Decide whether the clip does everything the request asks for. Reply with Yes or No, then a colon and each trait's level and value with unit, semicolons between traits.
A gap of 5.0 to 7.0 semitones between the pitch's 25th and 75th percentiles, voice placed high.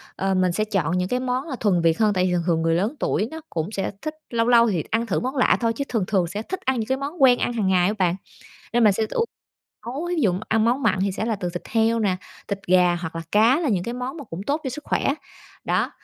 Yes: average, 5.3 semitones; high, 220 Hz